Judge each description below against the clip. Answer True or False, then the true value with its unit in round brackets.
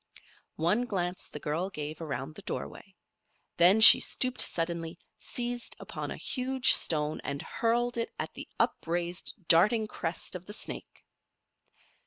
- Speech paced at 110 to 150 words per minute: True (140 wpm)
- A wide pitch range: True (5.8 semitones)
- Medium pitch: True (180 Hz)